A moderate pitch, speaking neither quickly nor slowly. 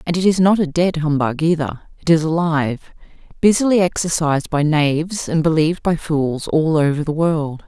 Yes: medium, 160 Hz; average, 180 wpm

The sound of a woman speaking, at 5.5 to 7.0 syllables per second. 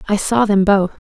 No: female; 5.0 syllables/s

